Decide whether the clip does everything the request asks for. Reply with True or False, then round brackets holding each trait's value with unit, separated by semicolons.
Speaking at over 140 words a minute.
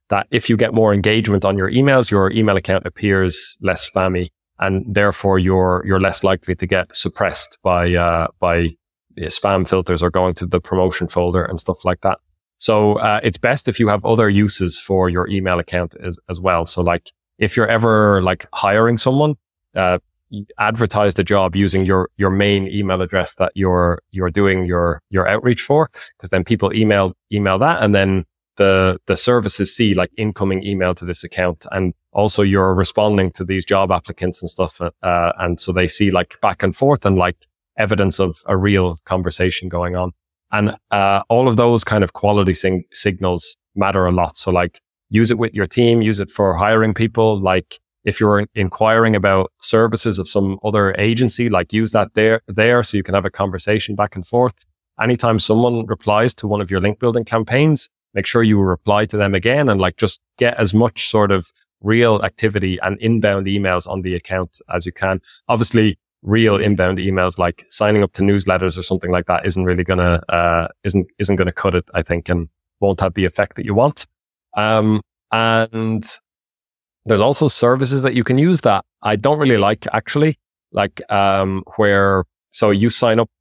True (195 wpm)